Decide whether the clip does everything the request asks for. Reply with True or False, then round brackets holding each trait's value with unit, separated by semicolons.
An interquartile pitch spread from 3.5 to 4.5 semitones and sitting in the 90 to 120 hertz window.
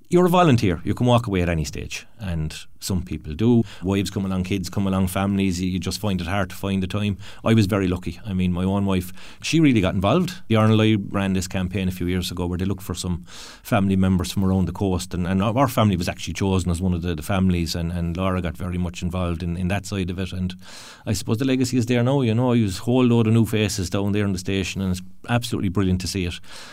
False (2.7 semitones; 95 Hz)